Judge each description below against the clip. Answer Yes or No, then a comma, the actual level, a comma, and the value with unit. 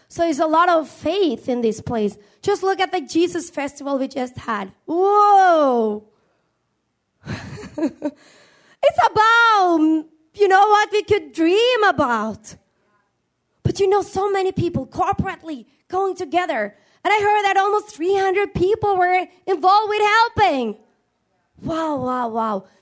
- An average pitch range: No, wide, 5.9 semitones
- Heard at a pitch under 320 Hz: No, very high, 345 Hz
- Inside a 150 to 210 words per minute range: No, slow, 135 wpm